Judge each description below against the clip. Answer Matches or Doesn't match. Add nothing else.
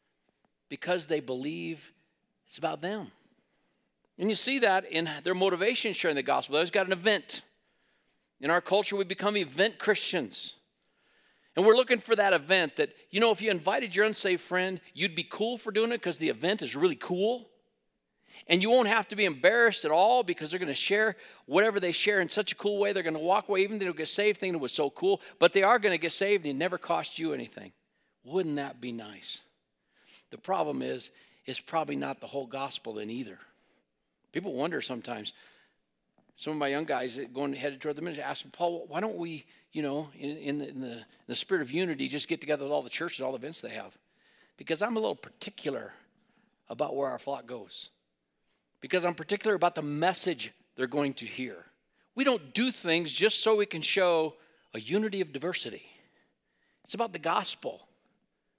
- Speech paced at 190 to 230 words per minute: Matches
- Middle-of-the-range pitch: Matches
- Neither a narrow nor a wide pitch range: Doesn't match